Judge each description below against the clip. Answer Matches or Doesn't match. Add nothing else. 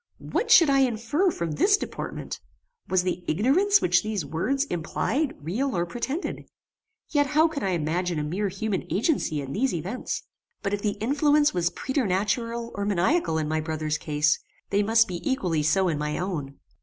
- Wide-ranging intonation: Matches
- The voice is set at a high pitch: Matches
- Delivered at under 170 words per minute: Doesn't match